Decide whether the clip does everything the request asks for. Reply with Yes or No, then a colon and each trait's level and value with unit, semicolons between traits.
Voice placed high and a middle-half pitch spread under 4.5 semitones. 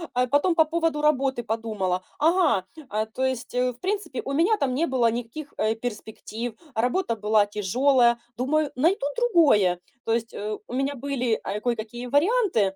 No: very high, 250 Hz; average, 5.2 semitones